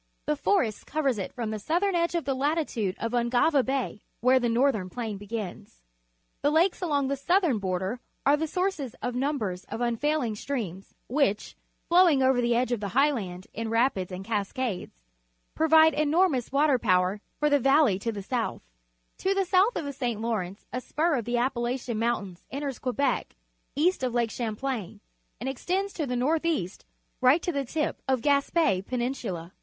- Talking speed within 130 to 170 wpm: No, average, 180 wpm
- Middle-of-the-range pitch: No, very high, 255 Hz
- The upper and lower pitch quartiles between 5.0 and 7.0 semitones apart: Yes, average, 5.3 semitones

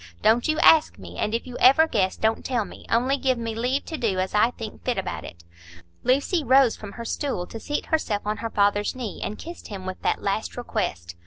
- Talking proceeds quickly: Yes, fast, 230 wpm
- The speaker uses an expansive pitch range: No, average, 4.2 semitones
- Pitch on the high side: Yes, high, 230 Hz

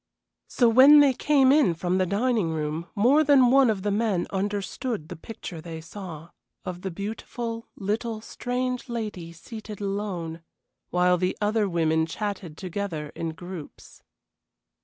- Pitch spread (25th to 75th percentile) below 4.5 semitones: No, average, 5.1 semitones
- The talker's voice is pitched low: No, high, 200 Hz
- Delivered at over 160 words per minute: No, average, 145 wpm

